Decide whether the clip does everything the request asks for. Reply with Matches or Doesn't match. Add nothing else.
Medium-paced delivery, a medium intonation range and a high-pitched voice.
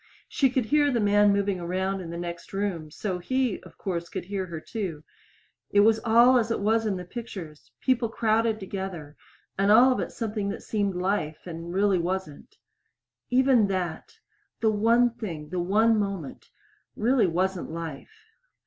Matches